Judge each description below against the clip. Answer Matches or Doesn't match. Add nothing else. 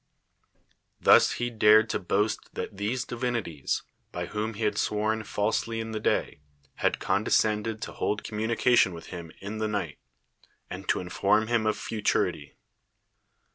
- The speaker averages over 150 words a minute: Doesn't match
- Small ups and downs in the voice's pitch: Matches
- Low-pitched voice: Matches